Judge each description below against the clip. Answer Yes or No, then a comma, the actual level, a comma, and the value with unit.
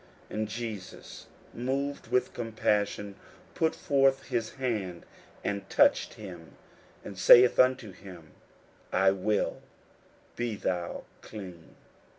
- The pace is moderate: No, slow, 110 wpm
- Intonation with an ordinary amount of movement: Yes, average, 4.4 semitones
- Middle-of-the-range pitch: No, low, 110 Hz